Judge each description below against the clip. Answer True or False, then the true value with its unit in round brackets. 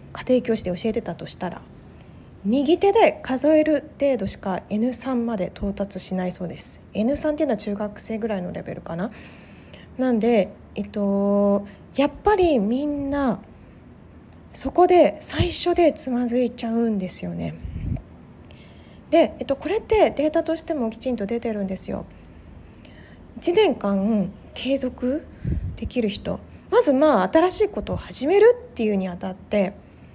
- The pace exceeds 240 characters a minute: True (260 characters per minute)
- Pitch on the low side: False (240 Hz)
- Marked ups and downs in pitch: True (6.8 semitones)